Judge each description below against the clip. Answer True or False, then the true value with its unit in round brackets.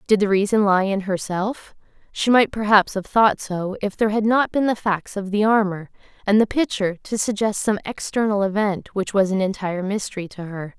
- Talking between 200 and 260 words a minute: True (205 wpm)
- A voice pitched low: False (205 Hz)